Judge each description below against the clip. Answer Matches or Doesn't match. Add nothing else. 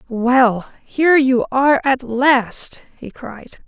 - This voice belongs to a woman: Matches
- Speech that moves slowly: Matches